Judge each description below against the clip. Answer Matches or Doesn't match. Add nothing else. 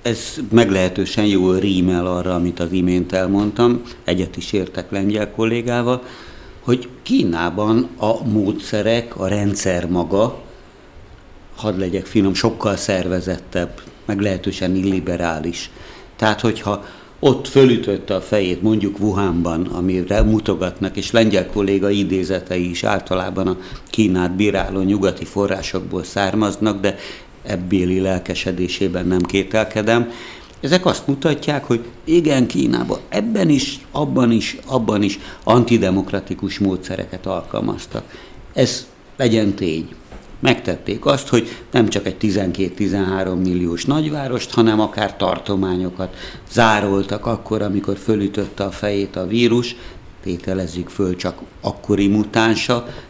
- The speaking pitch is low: Matches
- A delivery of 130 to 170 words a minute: Doesn't match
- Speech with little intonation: Doesn't match